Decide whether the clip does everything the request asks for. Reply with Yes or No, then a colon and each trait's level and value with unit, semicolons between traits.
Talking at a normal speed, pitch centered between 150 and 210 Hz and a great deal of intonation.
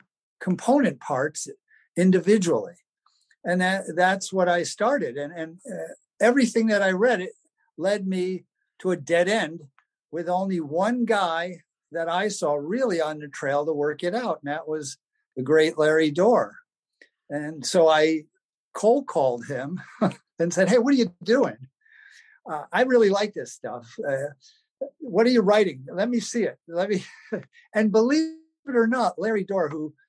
Yes: average, 165 wpm; medium, 185 Hz; wide, 6.7 semitones